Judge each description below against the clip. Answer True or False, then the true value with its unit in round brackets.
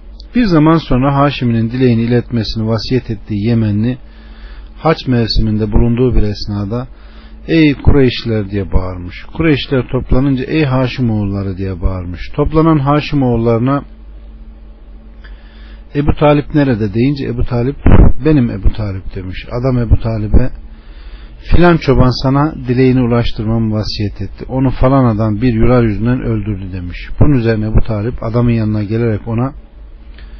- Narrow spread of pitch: False (4.1 semitones)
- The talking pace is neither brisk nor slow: True (125 wpm)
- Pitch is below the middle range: True (115 Hz)